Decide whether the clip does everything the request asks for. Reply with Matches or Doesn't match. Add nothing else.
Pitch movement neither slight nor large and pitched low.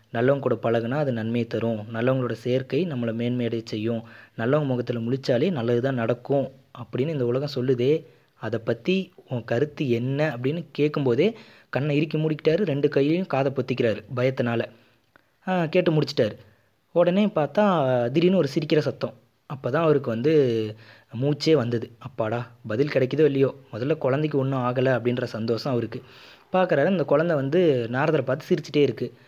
Matches